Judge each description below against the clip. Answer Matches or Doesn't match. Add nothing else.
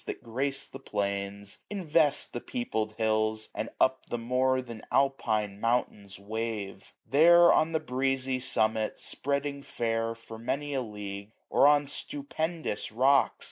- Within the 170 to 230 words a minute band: Doesn't match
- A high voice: Doesn't match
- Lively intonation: Doesn't match